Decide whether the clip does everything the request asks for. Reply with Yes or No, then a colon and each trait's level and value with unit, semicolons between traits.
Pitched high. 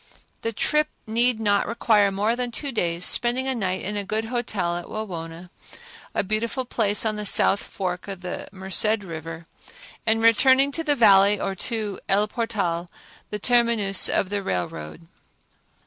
Yes: high, 210 Hz